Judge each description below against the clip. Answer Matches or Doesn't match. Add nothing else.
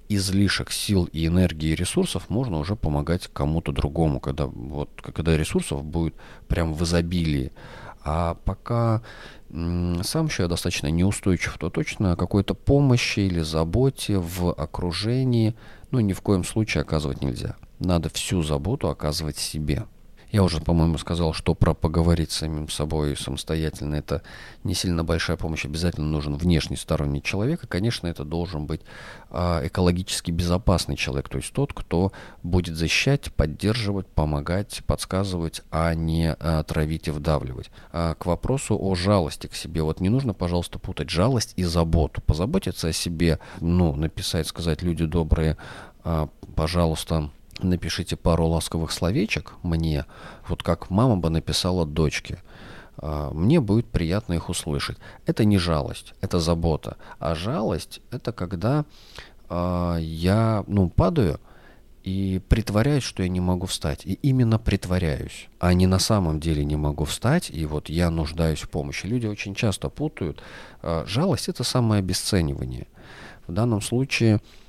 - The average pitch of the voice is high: Doesn't match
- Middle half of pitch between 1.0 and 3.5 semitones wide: Doesn't match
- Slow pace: Doesn't match